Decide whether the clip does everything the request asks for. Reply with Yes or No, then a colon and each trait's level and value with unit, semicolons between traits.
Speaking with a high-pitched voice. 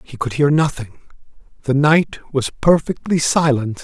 No: medium, 140 Hz